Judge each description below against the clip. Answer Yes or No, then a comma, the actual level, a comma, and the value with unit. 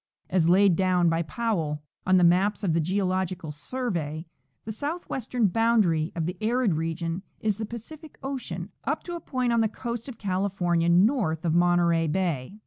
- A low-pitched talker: No, medium, 185 Hz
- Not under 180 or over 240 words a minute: No, average, 170 wpm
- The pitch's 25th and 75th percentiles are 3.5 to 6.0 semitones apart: Yes, average, 5.2 semitones